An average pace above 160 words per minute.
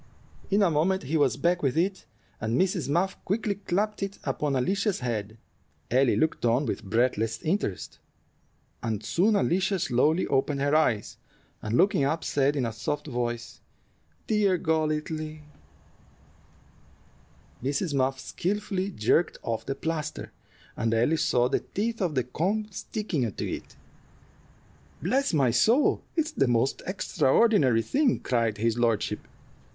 No: average, 140 wpm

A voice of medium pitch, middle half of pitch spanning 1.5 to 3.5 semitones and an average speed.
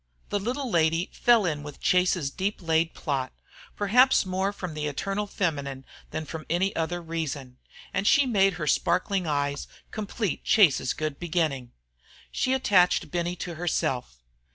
No: medium, 175 Hz; average, 4.7 semitones; average, 150 wpm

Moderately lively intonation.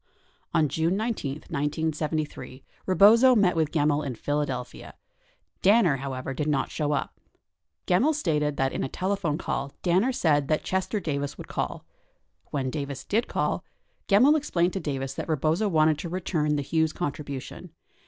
Yes: average, 4.6 semitones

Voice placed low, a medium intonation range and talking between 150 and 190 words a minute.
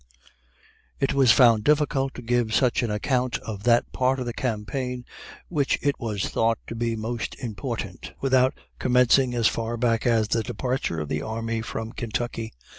No: low, 120 Hz; narrow, 2.3 semitones; average, 170 wpm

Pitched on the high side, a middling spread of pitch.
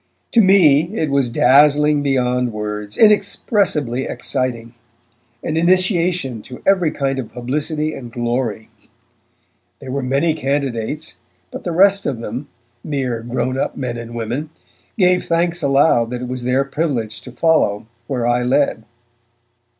No: low, 135 Hz; average, 4.6 semitones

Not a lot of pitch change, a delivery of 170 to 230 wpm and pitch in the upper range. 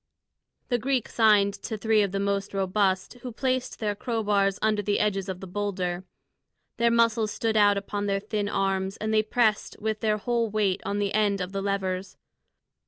Yes: narrow, 1.8 semitones; average, 190 wpm; high, 205 Hz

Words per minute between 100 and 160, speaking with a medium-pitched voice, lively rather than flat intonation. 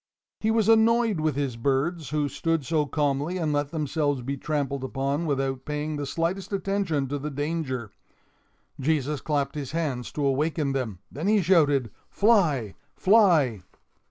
No: average, 155 wpm; medium, 150 Hz; average, 3.5 semitones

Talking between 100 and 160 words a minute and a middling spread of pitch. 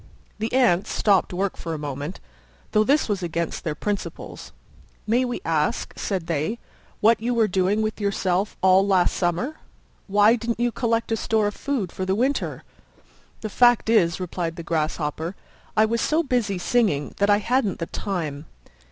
No: average, 170 wpm; average, 4.8 semitones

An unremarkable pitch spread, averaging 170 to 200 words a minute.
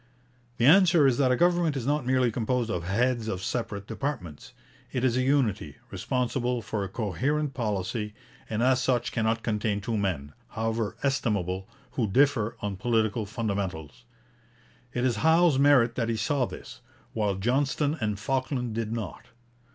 No: average, 4.0 semitones; average, 160 wpm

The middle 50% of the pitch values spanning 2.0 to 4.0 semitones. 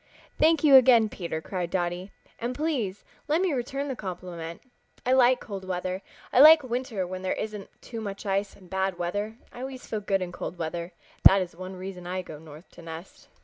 No: wide, 5.6 semitones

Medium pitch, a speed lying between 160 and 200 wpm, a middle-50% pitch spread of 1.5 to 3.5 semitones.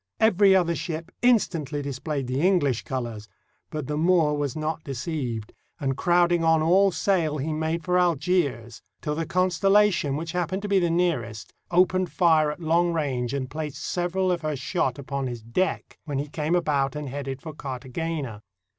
No: medium, 155 Hz; average, 175 wpm; average, 4.3 semitones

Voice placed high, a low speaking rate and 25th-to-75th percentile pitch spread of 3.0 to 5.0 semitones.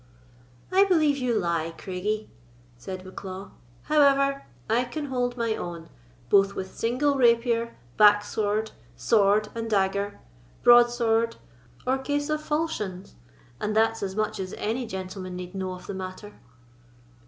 Yes: high, 215 Hz; slow, 130 wpm; average, 4.5 semitones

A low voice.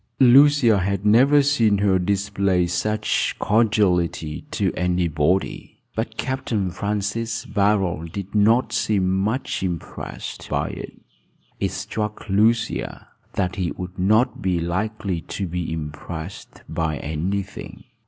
Yes: low, 100 Hz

